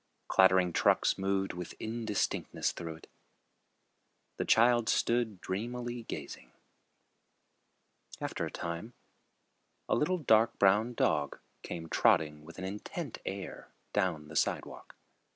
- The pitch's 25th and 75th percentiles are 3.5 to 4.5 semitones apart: No, average, 5.3 semitones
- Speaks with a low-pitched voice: Yes, low, 100 Hz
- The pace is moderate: No, slow, 115 wpm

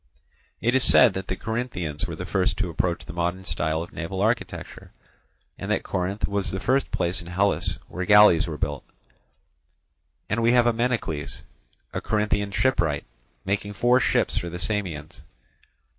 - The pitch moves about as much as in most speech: Yes, average, 4.0 semitones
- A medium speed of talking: Yes, average, 160 wpm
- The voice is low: Yes, very low, 95 Hz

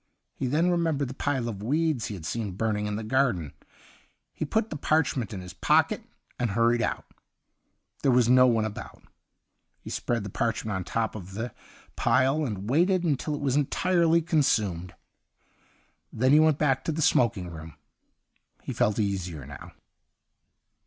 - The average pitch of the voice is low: Yes, low, 120 Hz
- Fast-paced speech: No, average, 170 wpm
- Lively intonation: Yes, wide, 6.1 semitones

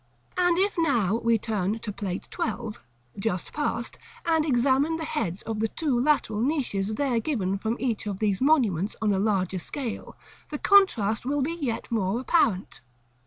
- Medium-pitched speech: No, high, 230 Hz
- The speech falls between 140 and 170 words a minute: Yes, average, 165 wpm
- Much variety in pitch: Yes, wide, 6.0 semitones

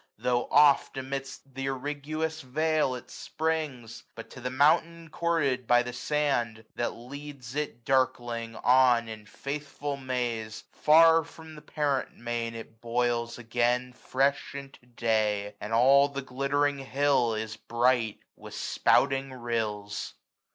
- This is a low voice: Yes, low, 130 Hz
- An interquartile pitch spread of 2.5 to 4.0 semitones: Yes, average, 3.4 semitones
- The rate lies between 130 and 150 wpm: Yes, slow, 135 wpm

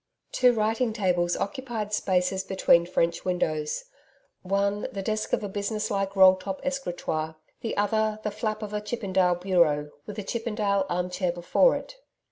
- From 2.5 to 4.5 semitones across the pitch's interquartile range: Yes, average, 3.0 semitones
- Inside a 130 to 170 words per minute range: Yes, average, 160 wpm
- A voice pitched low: No, high, 200 Hz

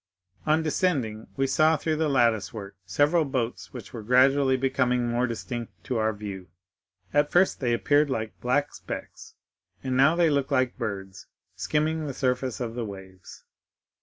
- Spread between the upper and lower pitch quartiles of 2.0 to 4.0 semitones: No, average, 4.6 semitones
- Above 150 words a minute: Yes, average, 165 wpm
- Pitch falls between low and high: No, low, 130 Hz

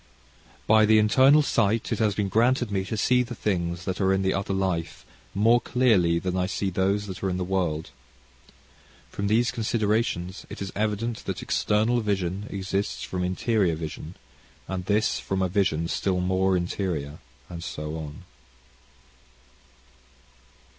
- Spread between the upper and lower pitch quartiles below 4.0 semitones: Yes, average, 3.1 semitones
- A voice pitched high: No, very low, 95 Hz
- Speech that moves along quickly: No, average, 155 wpm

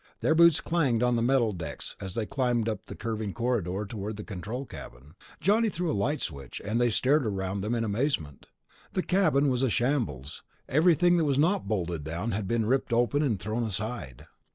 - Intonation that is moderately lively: No, wide, 5.8 semitones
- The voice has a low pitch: Yes, low, 115 Hz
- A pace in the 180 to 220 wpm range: Yes, average, 200 wpm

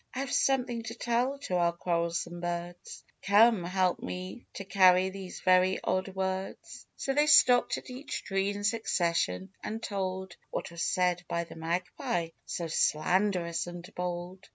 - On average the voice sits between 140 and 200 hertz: Yes, medium, 185 Hz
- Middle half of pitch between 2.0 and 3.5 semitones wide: Yes, average, 2.8 semitones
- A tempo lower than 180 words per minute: Yes, average, 155 wpm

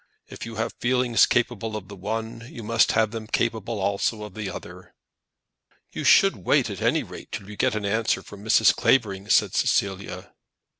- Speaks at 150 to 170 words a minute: No, average, 185 wpm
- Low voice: Yes, low, 110 Hz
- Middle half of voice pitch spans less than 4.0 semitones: Yes, narrow, 2.4 semitones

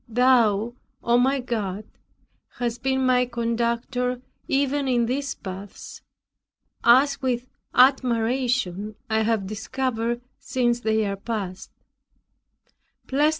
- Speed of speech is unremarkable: No, slow, 100 wpm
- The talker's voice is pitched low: No, high, 240 Hz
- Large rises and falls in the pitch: No, narrow, 2.6 semitones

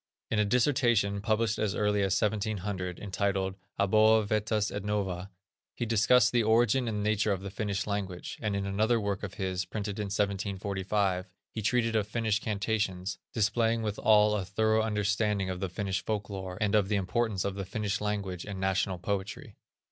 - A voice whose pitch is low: Yes, low, 105 Hz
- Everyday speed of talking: Yes, average, 175 wpm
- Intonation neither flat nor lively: No, narrow, 1.9 semitones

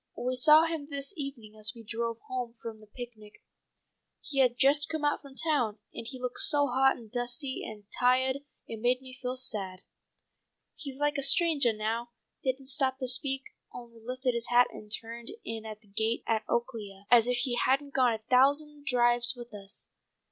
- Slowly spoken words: No, average, 190 wpm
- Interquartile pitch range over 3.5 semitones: No, average, 2.9 semitones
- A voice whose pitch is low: No, high, 245 Hz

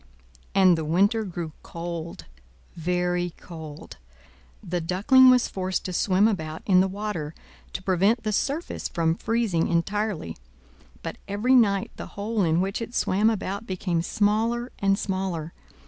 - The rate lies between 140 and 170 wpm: Yes, average, 145 wpm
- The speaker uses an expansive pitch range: No, average, 3.8 semitones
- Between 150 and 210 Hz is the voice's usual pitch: Yes, high, 190 Hz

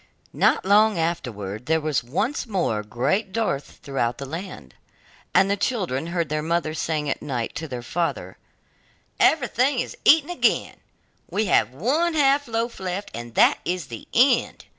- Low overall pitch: No, medium, 170 Hz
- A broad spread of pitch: Yes, wide, 8.8 semitones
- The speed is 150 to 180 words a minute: Yes, average, 160 wpm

